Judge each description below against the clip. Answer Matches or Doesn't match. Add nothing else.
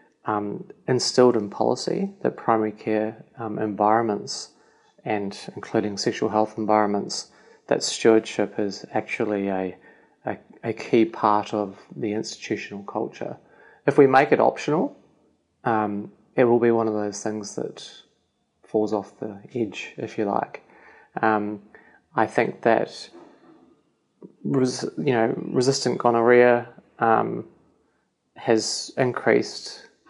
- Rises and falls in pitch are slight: Matches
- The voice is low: Matches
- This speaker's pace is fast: Doesn't match